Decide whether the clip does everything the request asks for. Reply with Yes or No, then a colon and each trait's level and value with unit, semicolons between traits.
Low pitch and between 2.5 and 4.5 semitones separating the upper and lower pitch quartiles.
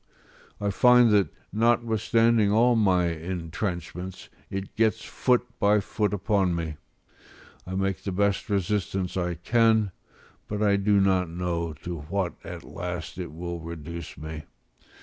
Yes: very low, 95 Hz; average, 3.4 semitones